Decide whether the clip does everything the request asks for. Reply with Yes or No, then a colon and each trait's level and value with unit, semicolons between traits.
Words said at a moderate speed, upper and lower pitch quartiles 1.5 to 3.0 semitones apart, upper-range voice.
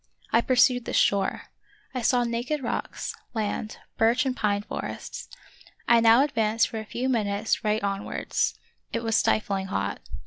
Yes: average, 160 wpm; narrow, 2.5 semitones; high, 225 Hz